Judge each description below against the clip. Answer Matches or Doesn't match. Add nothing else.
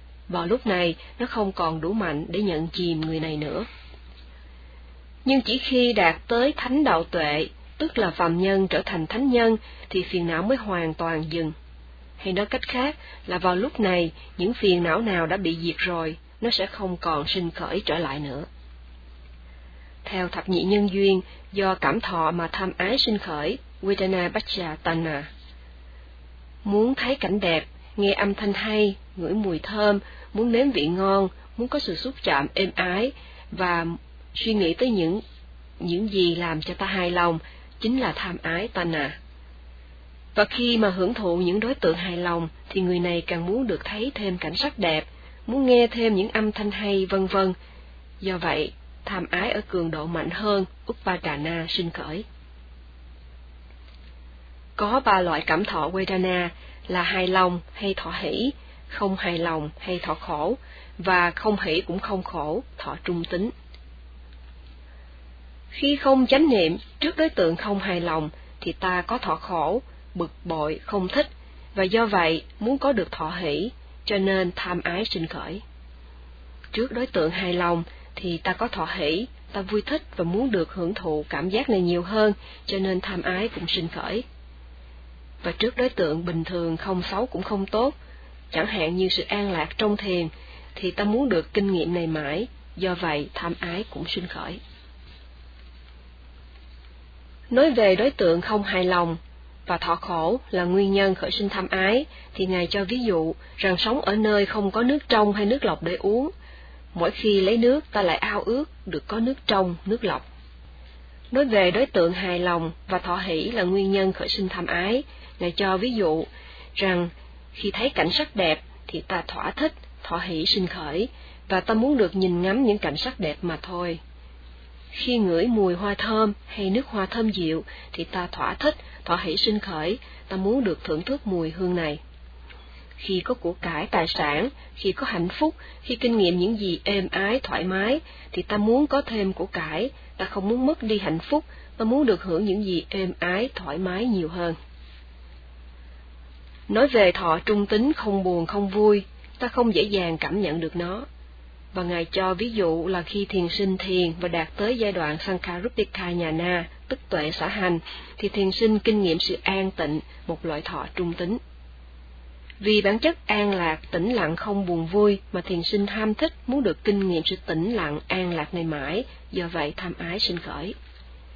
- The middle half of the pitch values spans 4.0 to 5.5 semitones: Matches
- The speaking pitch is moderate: Matches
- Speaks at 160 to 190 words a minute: Matches